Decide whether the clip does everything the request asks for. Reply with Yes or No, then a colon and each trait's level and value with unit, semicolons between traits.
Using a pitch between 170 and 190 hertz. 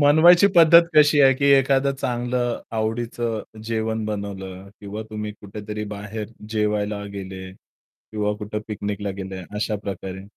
No: low, 105 Hz